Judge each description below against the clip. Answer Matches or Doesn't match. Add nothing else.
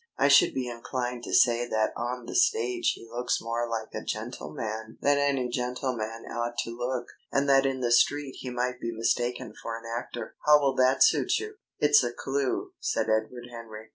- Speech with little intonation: Matches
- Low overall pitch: Matches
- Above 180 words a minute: Matches